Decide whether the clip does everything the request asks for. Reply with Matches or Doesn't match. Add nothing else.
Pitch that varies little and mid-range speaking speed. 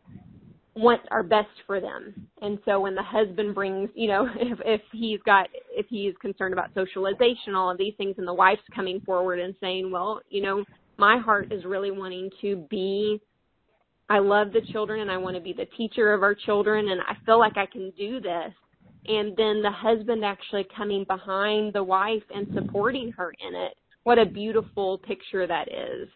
Matches